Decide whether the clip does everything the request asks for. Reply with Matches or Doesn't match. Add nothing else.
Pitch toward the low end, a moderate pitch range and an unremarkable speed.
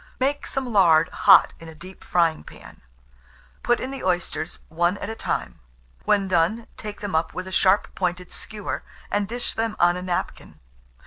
Doesn't match